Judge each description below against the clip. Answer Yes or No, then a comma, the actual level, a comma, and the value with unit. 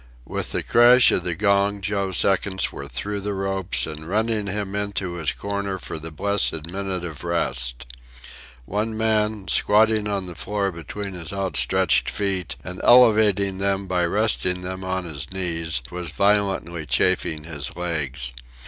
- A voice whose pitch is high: No, very low, 95 Hz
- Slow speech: No, average, 155 wpm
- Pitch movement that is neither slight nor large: Yes, average, 3.5 semitones